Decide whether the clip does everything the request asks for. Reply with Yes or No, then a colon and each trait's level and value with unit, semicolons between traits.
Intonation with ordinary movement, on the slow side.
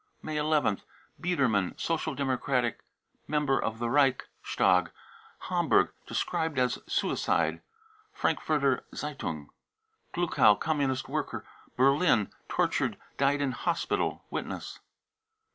Yes: average, 4.0 semitones; slow, 125 wpm